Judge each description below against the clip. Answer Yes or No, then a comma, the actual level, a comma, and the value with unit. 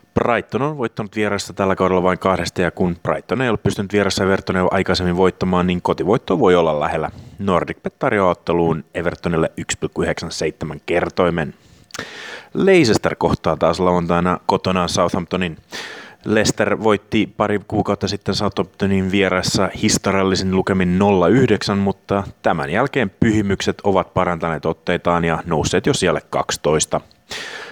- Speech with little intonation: Yes, narrow, 2.2 semitones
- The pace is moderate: Yes, average, 120 wpm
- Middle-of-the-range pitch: No, very low, 95 Hz